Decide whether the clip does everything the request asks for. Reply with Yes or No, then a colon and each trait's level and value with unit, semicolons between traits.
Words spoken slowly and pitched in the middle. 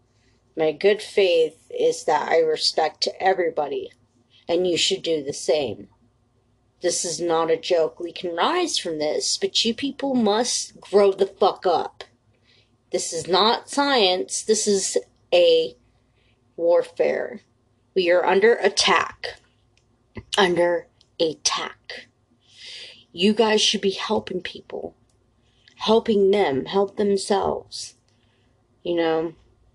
Yes: slow, 115 wpm; medium, 175 Hz